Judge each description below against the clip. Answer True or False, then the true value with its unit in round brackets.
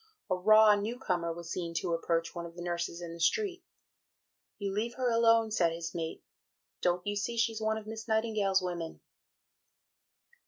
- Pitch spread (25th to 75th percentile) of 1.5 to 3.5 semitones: False (4.4 semitones)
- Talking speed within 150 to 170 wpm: False (180 wpm)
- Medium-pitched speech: False (195 Hz)